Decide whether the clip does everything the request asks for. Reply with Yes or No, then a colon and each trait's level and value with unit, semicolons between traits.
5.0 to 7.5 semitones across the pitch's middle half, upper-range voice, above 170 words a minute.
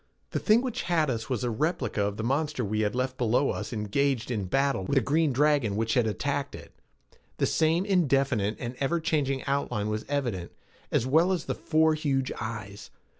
No: average, 5.3 semitones; low, 135 Hz; average, 195 wpm